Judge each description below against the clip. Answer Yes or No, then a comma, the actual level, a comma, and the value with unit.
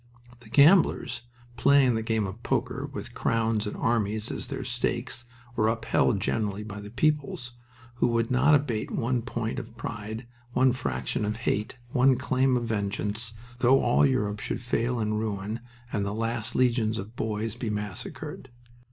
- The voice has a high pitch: No, low, 115 Hz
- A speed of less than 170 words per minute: Yes, average, 160 wpm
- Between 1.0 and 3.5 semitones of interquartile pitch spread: Yes, narrow, 2.6 semitones